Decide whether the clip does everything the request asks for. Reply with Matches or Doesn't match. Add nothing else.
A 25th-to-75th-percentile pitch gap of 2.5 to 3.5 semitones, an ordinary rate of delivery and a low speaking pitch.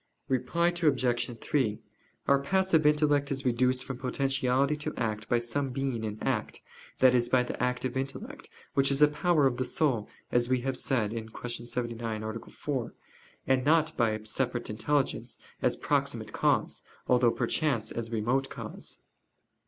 Matches